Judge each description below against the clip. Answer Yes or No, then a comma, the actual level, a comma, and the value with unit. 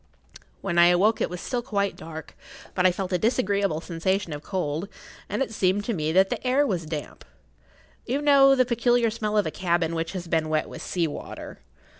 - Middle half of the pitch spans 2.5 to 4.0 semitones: No, average, 5.2 semitones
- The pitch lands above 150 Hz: Yes, high, 190 Hz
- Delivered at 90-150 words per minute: No, fast, 205 wpm